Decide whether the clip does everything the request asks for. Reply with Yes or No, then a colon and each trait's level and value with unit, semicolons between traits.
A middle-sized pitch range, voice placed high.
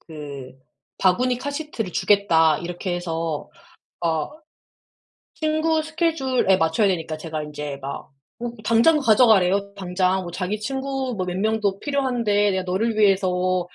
No: wide, 5.8 semitones; high, 195 Hz